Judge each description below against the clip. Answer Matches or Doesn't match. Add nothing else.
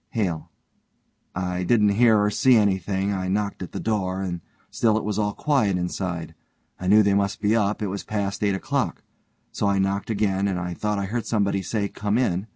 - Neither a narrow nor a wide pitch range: Doesn't match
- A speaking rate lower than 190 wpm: Doesn't match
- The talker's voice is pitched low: Matches